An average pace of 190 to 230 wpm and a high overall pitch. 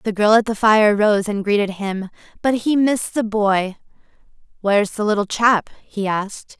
No: average, 180 wpm; high, 210 Hz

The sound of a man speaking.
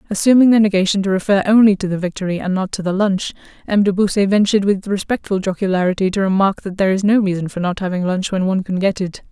No: female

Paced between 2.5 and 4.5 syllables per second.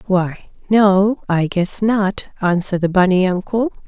Yes: 4.1 syllables/s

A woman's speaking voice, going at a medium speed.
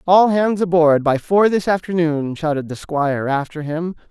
No: male; average, 175 wpm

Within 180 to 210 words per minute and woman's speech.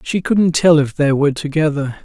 No: fast, 205 wpm; male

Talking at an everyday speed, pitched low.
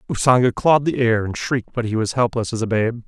No: fast, 255 wpm; low, 120 Hz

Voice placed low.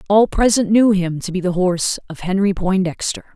No: high, 190 Hz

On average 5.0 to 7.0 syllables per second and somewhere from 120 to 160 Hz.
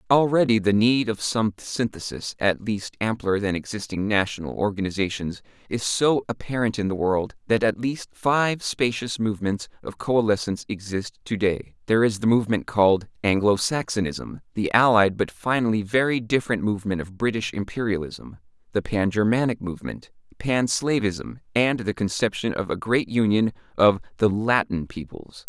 No: 5.1 syllables/s; low, 105 Hz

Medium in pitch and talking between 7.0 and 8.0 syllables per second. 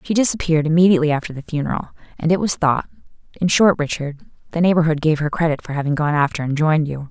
Yes: medium, 160 Hz; 7.1 syllables/s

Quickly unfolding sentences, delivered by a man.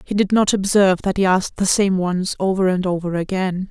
No: fast, 225 wpm; female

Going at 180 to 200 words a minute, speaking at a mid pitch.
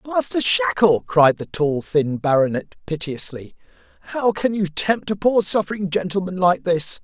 No: average, 155 wpm; medium, 170 Hz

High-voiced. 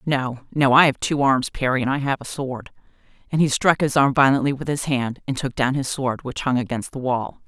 No: low, 135 Hz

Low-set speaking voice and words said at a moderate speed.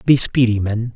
Yes: low, 115 Hz; average, 190 wpm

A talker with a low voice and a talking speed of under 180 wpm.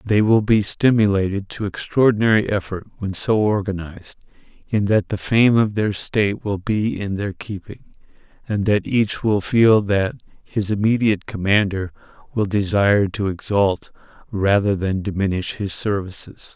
Yes: low, 100 Hz; average, 145 wpm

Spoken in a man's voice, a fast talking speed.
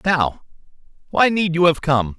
No: male; average, 165 wpm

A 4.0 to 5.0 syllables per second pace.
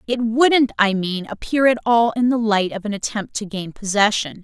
Yes: 4.8 syllables/s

